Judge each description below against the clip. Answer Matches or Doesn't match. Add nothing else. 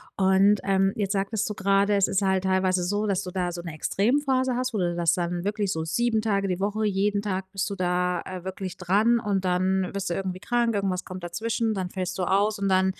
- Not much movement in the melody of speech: Matches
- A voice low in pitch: Doesn't match